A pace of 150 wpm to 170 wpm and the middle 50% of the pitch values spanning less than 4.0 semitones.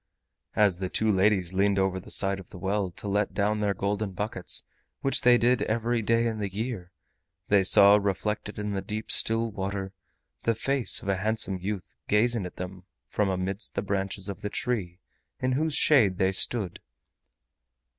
No: average, 180 wpm; narrow, 2.4 semitones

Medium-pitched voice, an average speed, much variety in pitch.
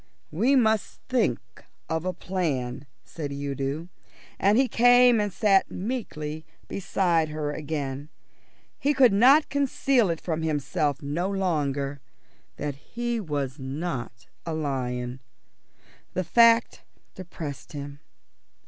No: medium, 160 Hz; slow, 110 wpm; wide, 6.5 semitones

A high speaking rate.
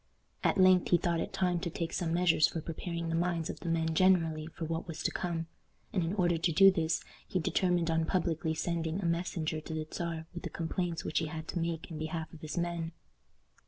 Yes: fast, 230 wpm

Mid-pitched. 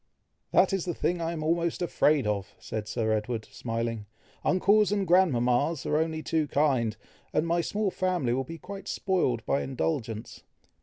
Yes: medium, 155 Hz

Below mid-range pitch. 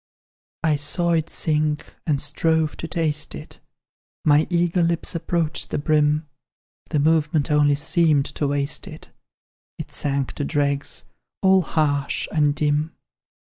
No: medium, 150 Hz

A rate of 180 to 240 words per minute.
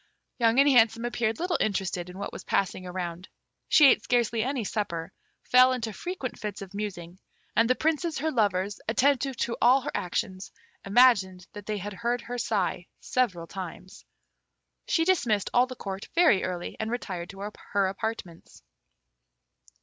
No: average, 155 wpm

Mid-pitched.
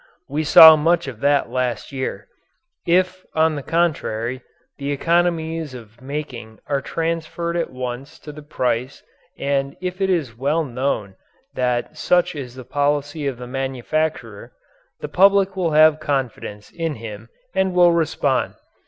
Yes: medium, 145 Hz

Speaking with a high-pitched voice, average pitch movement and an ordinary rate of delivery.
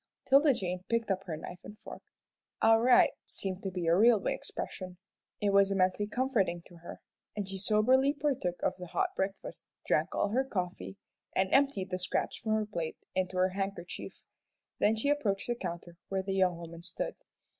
Yes: high, 195 Hz; average, 3.5 semitones; average, 185 wpm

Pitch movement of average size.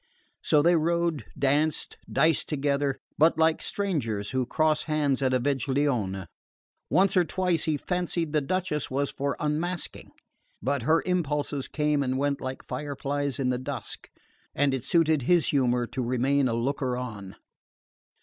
Yes: average, 3.4 semitones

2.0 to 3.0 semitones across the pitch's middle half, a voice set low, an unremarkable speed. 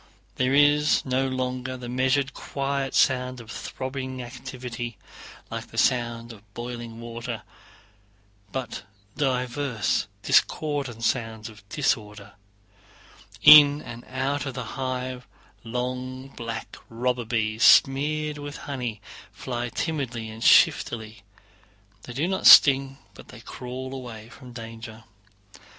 No: narrow, 2.4 semitones; low, 125 Hz; slow, 115 wpm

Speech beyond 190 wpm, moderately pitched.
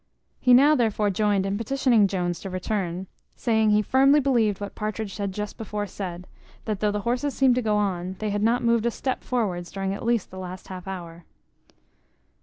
No: average, 200 wpm; high, 210 Hz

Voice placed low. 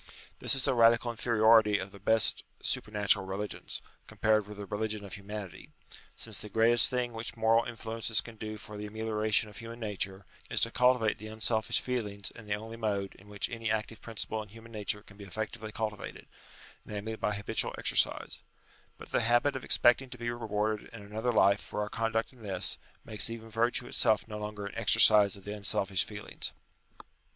Yes: low, 110 Hz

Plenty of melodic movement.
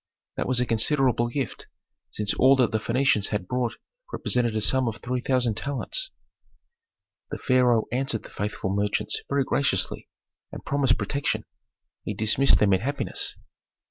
No: average, 3.7 semitones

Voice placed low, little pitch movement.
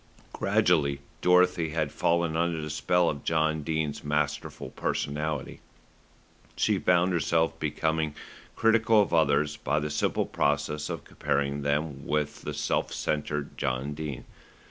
Yes: very low, 75 Hz; narrow, 2.0 semitones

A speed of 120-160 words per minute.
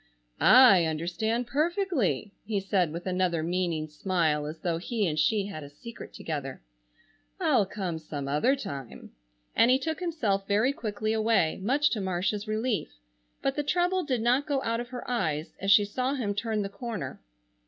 No: average, 175 wpm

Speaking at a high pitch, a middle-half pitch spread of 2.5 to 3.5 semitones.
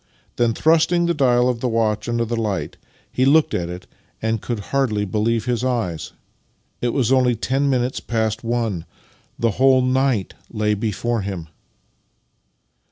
No: low, 120 Hz; average, 3.2 semitones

